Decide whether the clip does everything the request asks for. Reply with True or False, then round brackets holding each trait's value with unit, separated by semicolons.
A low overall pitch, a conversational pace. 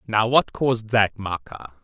True (110 Hz; 165 wpm)